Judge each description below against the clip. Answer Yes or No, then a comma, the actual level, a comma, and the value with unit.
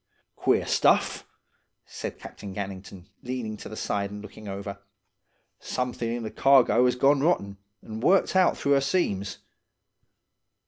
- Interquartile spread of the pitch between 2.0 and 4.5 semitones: No, average, 5.1 semitones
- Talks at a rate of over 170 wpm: No, average, 145 wpm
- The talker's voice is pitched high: No, low, 110 Hz